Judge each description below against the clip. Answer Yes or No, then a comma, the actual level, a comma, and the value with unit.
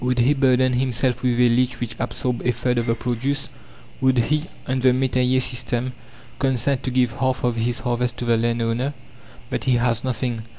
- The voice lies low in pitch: Yes, low, 125 Hz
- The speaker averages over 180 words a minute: Yes, average, 195 wpm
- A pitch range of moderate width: No, narrow, 1.4 semitones